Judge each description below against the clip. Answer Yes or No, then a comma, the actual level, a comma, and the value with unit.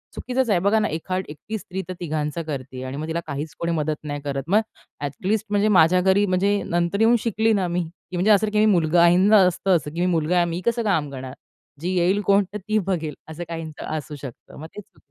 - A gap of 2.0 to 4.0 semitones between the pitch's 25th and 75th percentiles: No, average, 4.5 semitones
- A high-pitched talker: No, medium, 175 Hz